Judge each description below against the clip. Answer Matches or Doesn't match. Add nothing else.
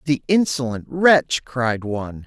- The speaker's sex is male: Matches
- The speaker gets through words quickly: Doesn't match